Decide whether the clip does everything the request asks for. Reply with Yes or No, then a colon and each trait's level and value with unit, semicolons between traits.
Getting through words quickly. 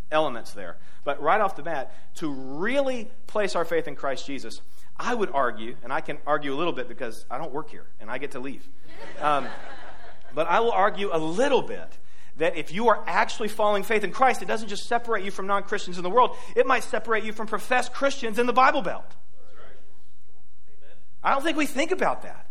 Yes: fast, 215 wpm